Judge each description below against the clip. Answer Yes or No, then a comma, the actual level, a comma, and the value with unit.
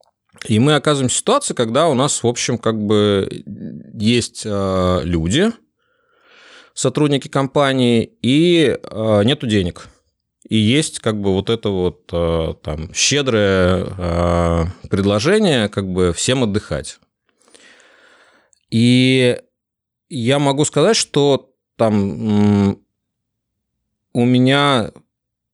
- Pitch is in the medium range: No, low, 115 Hz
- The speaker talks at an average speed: No, slow, 95 wpm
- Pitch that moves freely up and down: Yes, wide, 5.7 semitones